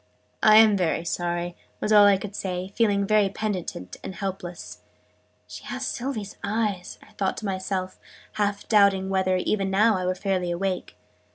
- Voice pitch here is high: Yes, high, 195 Hz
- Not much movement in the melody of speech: Yes, narrow, 2.1 semitones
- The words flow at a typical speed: Yes, average, 160 wpm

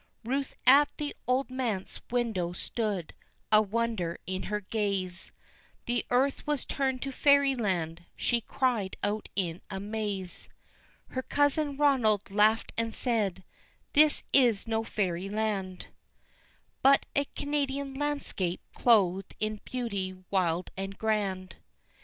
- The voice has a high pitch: Yes, high, 220 Hz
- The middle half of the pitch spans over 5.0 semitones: Yes, wide, 5.4 semitones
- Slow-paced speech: Yes, slow, 115 wpm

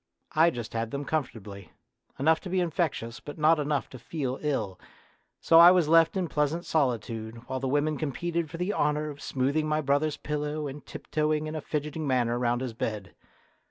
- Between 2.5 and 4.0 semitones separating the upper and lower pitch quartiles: Yes, average, 3.7 semitones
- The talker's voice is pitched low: No, medium, 150 Hz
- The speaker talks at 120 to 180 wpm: No, average, 190 wpm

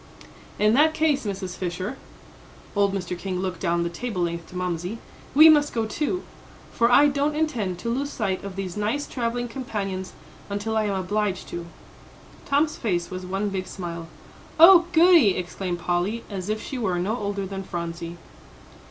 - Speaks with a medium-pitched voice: No, high, 200 Hz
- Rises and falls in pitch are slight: No, average, 5.1 semitones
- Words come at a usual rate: Yes, average, 170 wpm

